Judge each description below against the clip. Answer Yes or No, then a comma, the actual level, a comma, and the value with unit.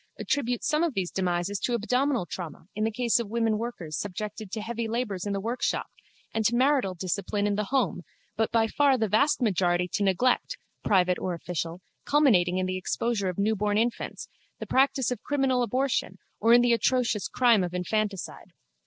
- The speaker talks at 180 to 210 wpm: Yes, average, 185 wpm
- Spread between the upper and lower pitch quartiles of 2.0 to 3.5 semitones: No, average, 4.5 semitones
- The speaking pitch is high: Yes, high, 215 Hz